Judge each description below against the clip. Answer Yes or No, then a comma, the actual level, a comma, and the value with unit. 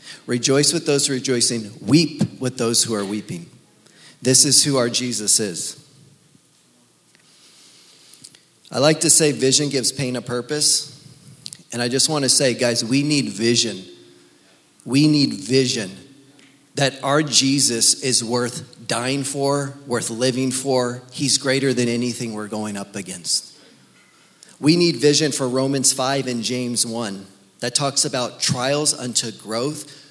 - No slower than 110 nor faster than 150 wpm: Yes, average, 140 wpm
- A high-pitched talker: No, low, 130 Hz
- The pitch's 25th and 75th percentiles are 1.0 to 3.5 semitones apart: Yes, average, 3.2 semitones